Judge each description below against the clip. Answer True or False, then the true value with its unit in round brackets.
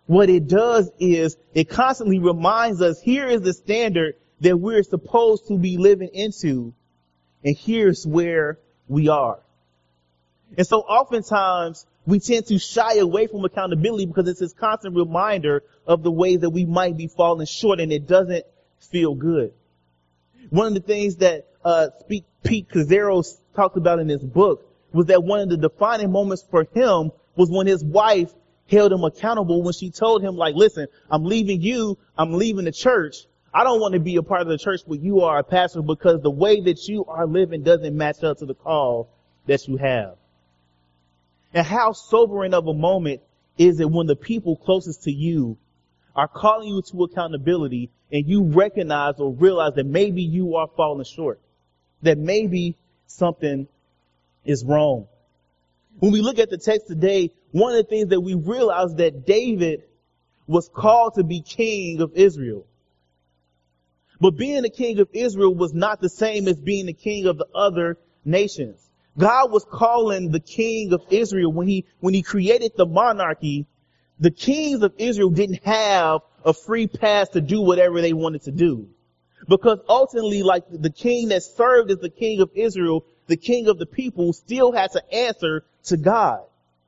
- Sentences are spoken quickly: False (175 wpm)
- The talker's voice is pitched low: False (180 Hz)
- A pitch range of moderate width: True (4.7 semitones)